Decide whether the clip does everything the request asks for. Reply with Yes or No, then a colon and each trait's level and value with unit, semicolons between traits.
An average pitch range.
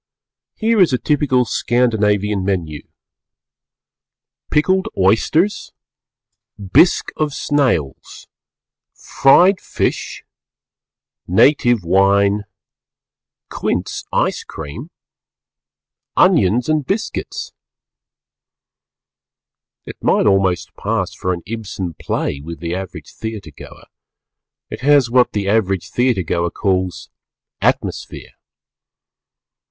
No: wide, 6.6 semitones